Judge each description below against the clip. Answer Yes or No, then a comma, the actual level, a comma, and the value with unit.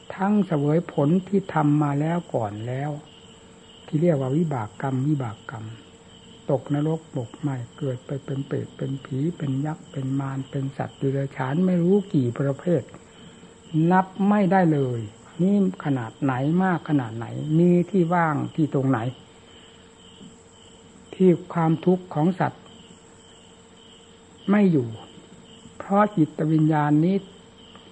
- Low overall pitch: No, medium, 150 Hz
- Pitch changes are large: No, average, 4.5 semitones